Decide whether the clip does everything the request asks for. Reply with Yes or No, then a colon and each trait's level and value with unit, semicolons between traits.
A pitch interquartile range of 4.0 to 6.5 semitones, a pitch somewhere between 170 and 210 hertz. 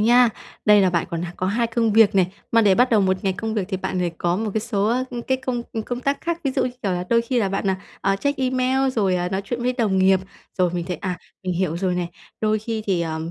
Yes: average, 4.4 semitones; high, 205 Hz